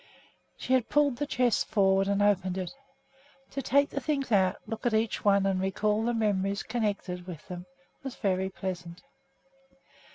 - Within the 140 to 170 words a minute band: Yes, average, 165 wpm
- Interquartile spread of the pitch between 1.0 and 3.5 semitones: No, average, 4.1 semitones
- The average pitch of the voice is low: No, high, 200 Hz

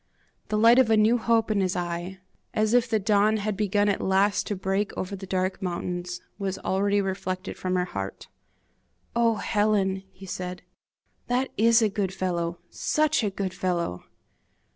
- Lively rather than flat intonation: No, narrow, 2.6 semitones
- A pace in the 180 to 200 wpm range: No, average, 170 wpm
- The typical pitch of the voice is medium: No, high, 195 Hz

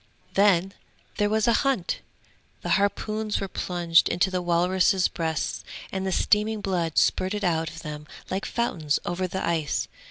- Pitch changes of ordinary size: Yes, average, 3.4 semitones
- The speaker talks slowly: No, average, 155 wpm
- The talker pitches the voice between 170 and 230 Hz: Yes, medium, 185 Hz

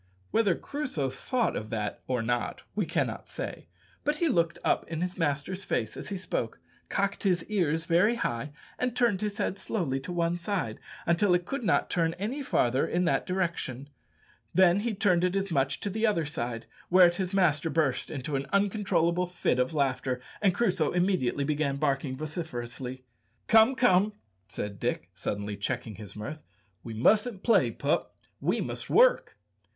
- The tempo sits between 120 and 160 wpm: No, average, 170 wpm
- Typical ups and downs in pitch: No, wide, 6.6 semitones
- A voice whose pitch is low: No, medium, 170 Hz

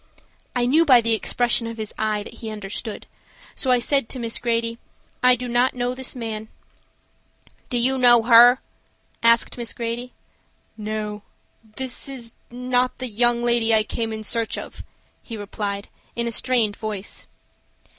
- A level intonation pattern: Yes, narrow, 2.1 semitones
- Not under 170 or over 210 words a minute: No, average, 160 wpm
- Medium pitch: No, high, 235 Hz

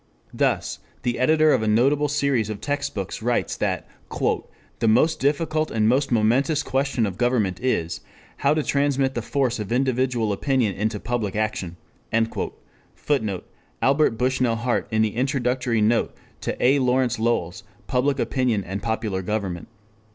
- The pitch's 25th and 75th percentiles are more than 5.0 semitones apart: No, average, 4.0 semitones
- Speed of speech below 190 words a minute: Yes, average, 150 wpm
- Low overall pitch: Yes, low, 120 Hz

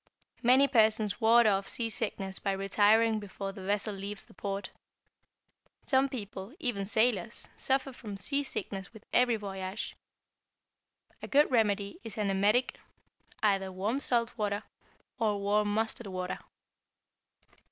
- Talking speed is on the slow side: Yes, slow, 125 wpm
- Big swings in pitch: No, average, 2.9 semitones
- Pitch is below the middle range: No, high, 210 Hz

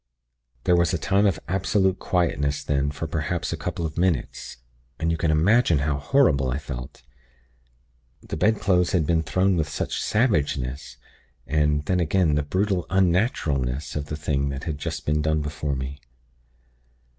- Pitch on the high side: No, very low, 80 Hz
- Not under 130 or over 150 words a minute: No, average, 160 wpm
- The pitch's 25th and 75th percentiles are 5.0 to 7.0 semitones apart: No, average, 4.0 semitones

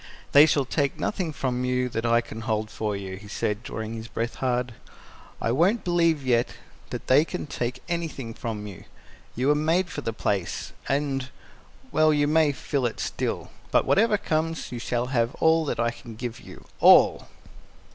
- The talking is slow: No, average, 185 wpm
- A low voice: Yes, low, 125 Hz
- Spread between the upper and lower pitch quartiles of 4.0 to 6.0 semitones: Yes, average, 5.1 semitones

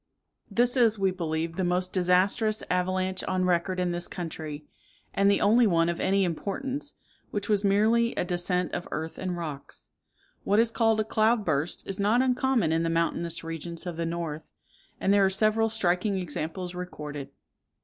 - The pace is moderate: Yes, average, 175 wpm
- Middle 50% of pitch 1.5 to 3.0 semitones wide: No, average, 3.9 semitones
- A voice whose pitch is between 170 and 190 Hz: Yes, medium, 185 Hz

